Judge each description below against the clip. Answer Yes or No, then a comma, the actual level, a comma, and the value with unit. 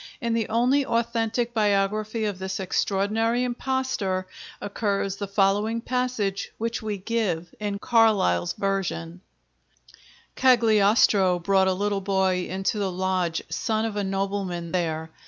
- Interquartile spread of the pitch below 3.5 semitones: Yes, average, 3.1 semitones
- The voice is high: Yes, high, 200 Hz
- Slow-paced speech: Yes, slow, 125 wpm